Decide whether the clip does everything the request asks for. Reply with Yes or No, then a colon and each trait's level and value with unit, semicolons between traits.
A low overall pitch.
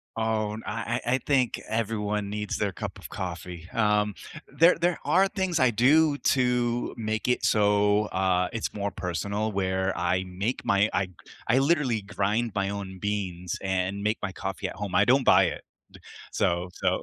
Yes: low, 105 Hz